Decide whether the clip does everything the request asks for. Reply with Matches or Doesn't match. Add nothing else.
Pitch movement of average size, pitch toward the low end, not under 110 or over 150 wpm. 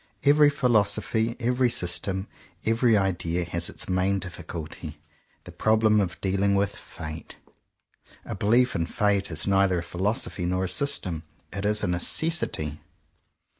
Matches